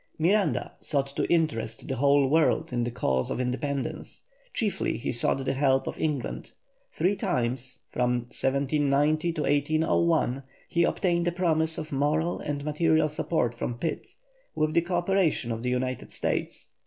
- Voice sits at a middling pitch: Yes, medium, 145 Hz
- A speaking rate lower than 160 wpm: Yes, average, 150 wpm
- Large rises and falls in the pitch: No, average, 4.1 semitones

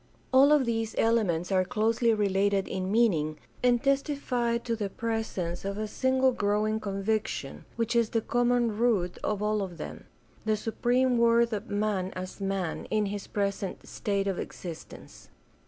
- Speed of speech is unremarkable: Yes, average, 160 wpm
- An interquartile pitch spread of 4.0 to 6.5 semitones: No, average, 3.1 semitones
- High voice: Yes, high, 215 Hz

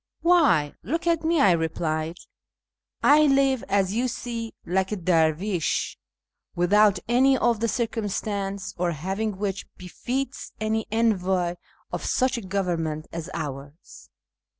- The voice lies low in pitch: No, high, 200 Hz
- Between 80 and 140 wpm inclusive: Yes, slow, 135 wpm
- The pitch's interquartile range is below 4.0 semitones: No, wide, 5.4 semitones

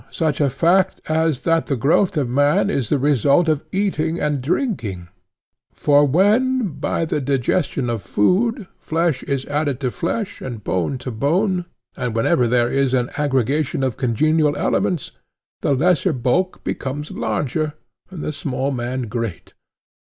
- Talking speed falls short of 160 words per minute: Yes, average, 150 wpm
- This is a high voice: No, medium, 145 Hz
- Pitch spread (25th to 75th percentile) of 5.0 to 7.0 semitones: No, average, 4.6 semitones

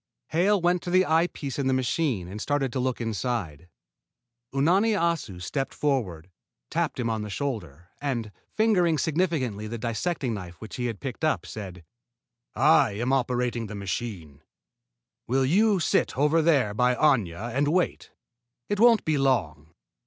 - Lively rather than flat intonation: Yes, wide, 6.9 semitones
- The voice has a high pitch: No, low, 130 Hz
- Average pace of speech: Yes, average, 160 wpm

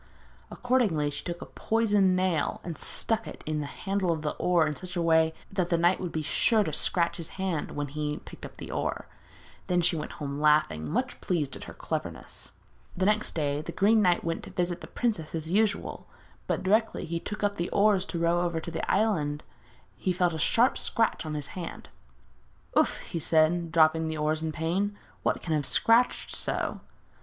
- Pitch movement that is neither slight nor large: Yes, average, 3.6 semitones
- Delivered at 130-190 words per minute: No, fast, 205 wpm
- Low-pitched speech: No, medium, 170 Hz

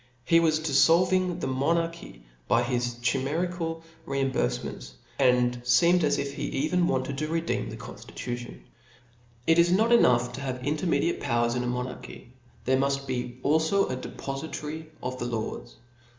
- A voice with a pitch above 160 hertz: No, medium, 140 Hz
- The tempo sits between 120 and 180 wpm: Yes, average, 155 wpm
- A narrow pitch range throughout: No, average, 4.9 semitones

